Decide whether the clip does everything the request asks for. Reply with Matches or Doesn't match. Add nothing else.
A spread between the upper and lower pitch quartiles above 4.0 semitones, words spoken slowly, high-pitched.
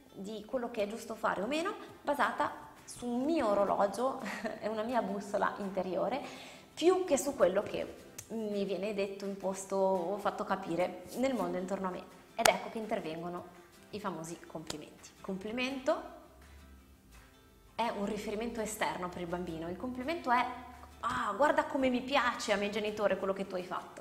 Doesn't match